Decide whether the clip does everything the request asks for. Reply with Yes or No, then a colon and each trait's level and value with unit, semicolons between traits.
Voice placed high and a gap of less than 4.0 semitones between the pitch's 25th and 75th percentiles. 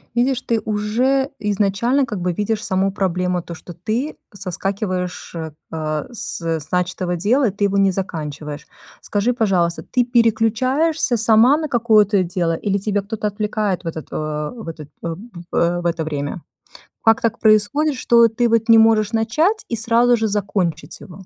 No: high, 205 Hz; average, 4.3 semitones